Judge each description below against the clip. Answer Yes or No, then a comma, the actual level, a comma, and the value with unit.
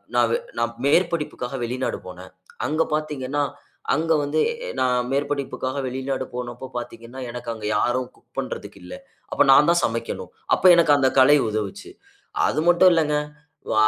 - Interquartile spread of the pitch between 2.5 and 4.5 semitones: Yes, average, 3.9 semitones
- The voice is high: No, low, 130 Hz